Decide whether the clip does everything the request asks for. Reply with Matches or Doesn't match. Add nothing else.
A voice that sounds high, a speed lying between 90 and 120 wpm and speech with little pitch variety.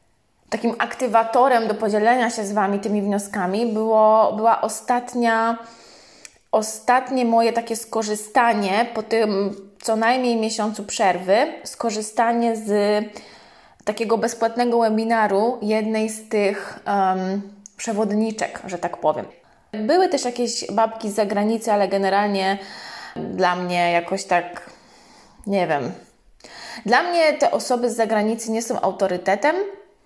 Matches